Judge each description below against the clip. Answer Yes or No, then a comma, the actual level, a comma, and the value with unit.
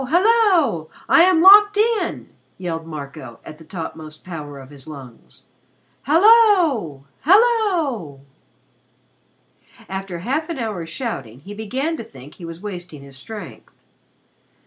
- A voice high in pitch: Yes, high, 200 Hz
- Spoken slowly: Yes, slow, 125 wpm